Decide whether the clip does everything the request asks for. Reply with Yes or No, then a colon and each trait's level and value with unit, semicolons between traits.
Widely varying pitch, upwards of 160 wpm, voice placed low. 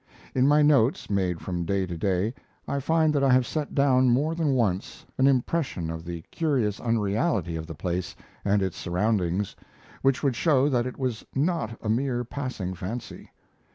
Yes: wide, 6.7 semitones; average, 180 wpm; low, 120 Hz